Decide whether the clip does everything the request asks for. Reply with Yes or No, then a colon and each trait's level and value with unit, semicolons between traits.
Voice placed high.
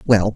No: low, 105 Hz